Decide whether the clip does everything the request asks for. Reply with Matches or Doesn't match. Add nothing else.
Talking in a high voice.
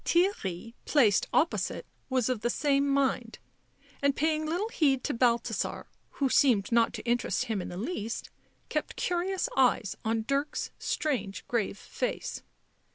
Matches